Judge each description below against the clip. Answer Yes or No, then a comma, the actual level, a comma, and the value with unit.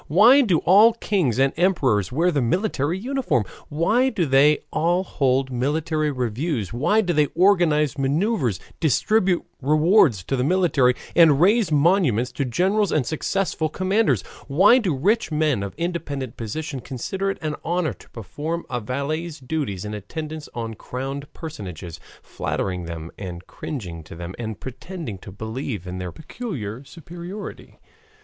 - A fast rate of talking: No, average, 150 wpm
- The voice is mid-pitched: Yes, medium, 150 Hz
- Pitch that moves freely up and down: Yes, wide, 6.5 semitones